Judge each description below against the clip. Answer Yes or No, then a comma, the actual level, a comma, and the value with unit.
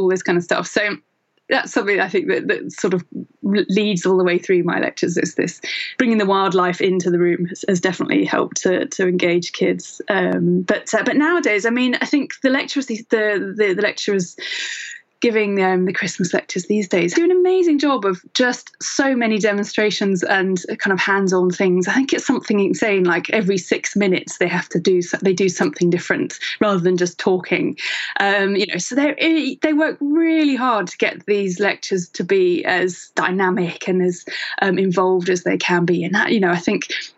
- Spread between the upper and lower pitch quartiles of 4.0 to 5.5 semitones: Yes, average, 5.1 semitones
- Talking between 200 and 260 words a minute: Yes, fast, 205 wpm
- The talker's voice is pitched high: Yes, high, 195 Hz